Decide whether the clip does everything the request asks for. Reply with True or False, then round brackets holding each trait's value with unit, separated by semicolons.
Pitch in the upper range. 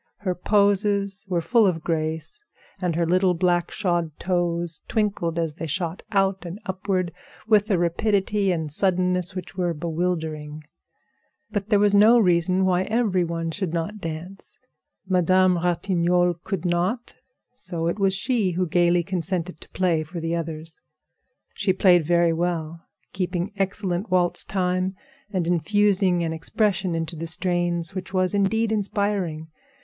False (180 Hz)